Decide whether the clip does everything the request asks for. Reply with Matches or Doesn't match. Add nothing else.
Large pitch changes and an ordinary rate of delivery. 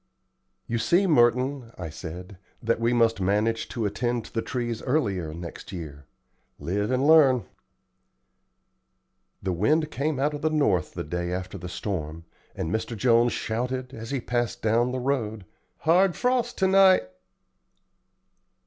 Matches